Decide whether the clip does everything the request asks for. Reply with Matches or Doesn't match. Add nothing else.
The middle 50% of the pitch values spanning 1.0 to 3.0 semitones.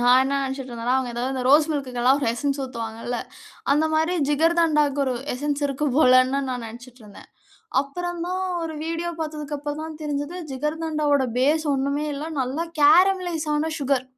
Doesn't match